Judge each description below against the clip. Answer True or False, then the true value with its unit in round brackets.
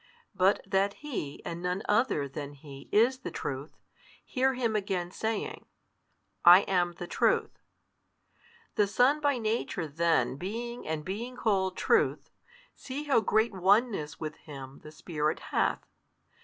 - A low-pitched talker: False (190 Hz)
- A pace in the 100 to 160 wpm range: True (140 wpm)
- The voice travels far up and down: True (6.7 semitones)